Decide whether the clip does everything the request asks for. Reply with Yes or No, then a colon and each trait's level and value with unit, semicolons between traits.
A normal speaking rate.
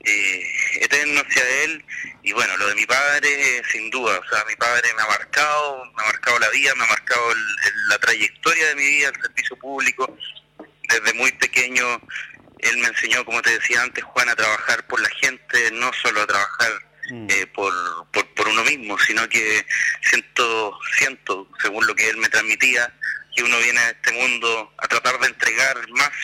No: fast, 195 wpm